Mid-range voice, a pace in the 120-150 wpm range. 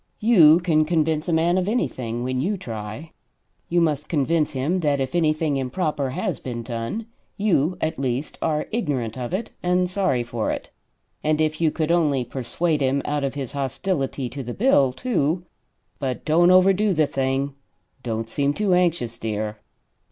No: medium, 150 Hz; average, 170 wpm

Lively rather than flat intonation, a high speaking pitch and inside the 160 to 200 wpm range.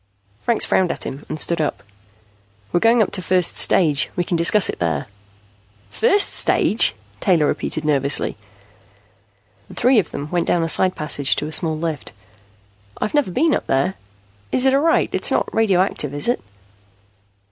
No: wide, 6.4 semitones; medium, 175 Hz; average, 170 wpm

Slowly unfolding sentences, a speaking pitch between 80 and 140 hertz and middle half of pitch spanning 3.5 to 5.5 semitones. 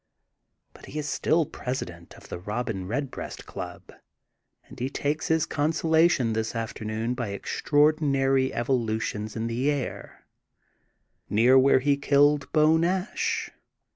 Yes: slow, 130 wpm; low, 135 Hz; average, 4.7 semitones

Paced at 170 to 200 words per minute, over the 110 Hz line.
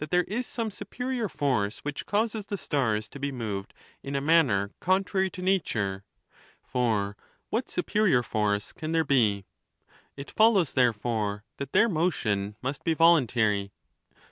No: average, 155 wpm; medium, 140 Hz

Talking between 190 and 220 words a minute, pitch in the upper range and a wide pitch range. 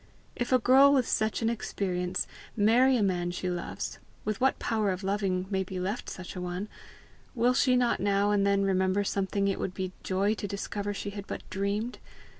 No: average, 200 wpm; high, 200 Hz; average, 2.7 semitones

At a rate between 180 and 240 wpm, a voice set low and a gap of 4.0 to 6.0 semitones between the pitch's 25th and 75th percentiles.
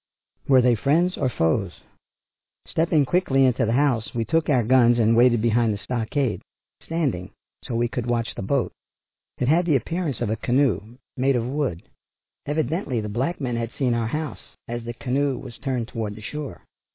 No: average, 185 wpm; low, 125 Hz; average, 3.6 semitones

